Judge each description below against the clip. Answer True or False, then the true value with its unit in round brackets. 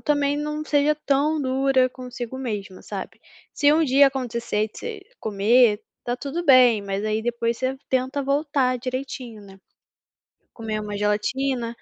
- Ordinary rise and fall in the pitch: True (3.9 semitones)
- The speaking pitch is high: True (255 Hz)